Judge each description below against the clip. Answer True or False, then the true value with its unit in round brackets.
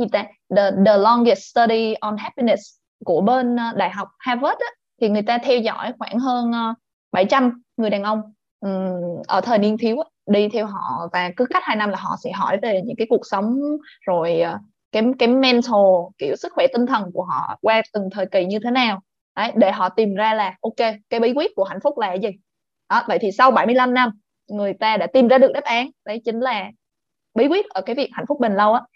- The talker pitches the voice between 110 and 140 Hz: False (225 Hz)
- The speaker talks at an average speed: True (220 wpm)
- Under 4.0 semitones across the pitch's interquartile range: True (3.6 semitones)